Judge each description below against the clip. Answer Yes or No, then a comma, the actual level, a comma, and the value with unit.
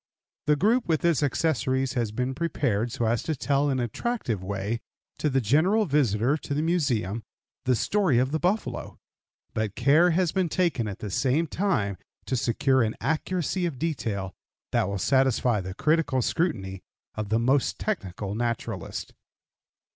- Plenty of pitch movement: Yes, wide, 6.4 semitones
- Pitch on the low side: Yes, low, 130 Hz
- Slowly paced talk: No, average, 160 wpm